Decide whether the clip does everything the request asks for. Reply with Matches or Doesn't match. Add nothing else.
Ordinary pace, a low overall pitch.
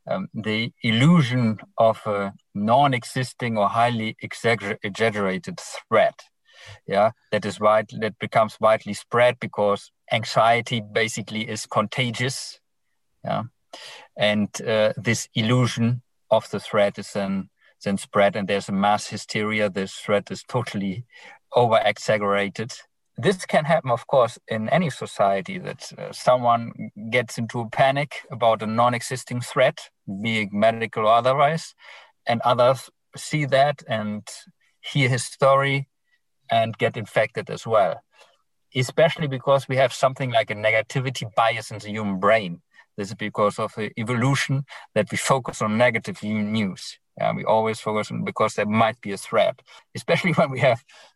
Matches